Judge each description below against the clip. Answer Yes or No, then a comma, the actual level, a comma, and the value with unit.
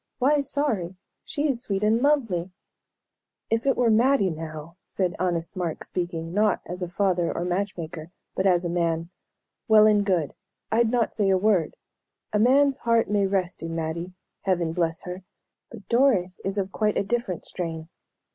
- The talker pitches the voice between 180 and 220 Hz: Yes, high, 190 Hz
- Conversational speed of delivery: Yes, average, 175 wpm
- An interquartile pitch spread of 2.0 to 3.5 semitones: No, average, 4.6 semitones